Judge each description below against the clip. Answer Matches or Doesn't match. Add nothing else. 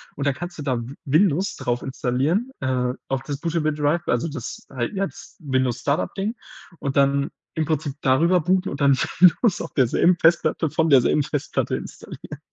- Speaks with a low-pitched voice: Doesn't match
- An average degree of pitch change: Matches